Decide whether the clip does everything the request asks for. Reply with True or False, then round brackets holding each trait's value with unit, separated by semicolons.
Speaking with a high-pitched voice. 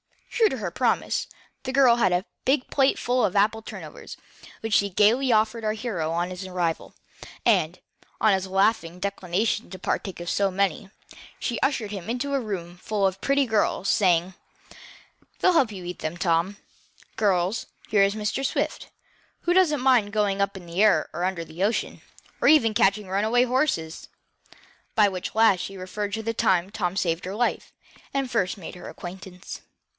True (200 Hz)